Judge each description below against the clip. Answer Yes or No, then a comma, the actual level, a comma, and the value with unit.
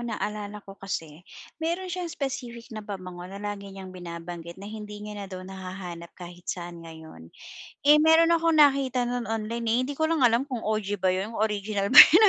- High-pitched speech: Yes, high, 210 Hz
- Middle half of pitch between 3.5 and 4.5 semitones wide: No, average, 5.0 semitones